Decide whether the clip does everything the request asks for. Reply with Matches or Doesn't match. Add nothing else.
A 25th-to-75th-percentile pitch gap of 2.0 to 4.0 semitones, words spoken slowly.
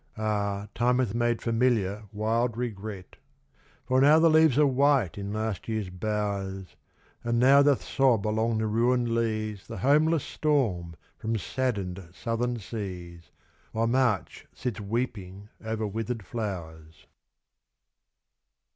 Matches